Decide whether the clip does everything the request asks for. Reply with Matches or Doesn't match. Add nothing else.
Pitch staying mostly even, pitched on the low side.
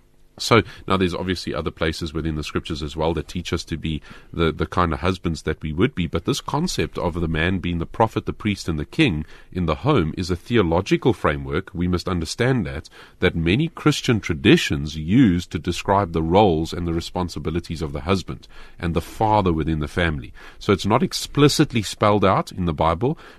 Doesn't match